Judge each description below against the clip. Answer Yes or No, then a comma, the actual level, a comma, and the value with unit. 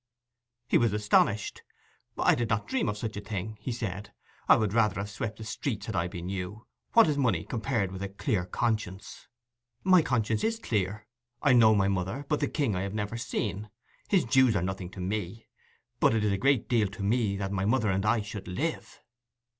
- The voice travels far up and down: No, average, 3.2 semitones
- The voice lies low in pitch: Yes, low, 105 Hz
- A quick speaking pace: Yes, fast, 210 wpm